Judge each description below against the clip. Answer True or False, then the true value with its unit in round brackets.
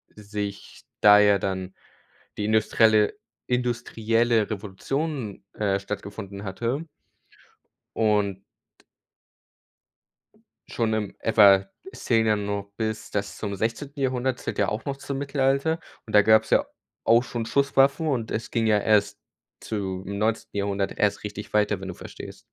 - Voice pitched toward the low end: True (110 Hz)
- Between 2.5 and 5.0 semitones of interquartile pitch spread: True (2.8 semitones)